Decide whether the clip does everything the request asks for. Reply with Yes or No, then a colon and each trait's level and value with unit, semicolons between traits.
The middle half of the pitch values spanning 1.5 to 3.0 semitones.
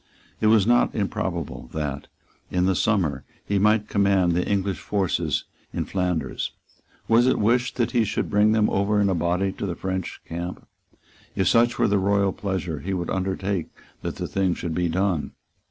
Yes: average, 2.7 semitones